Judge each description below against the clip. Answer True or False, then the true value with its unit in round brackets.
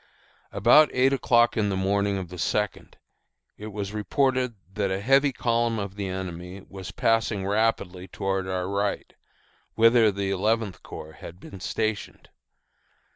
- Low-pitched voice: True (100 Hz)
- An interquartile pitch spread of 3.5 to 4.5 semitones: False (3.1 semitones)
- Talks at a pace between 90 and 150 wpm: True (145 wpm)